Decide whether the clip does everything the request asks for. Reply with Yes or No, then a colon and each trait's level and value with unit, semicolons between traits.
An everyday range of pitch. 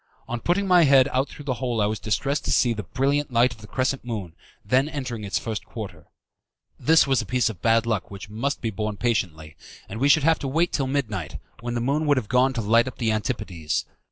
Yes: average, 4.1 semitones